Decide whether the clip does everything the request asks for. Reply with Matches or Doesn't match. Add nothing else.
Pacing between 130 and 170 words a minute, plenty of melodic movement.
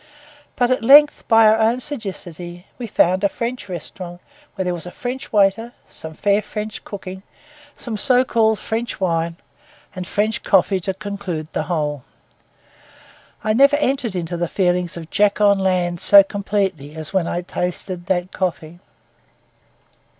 Doesn't match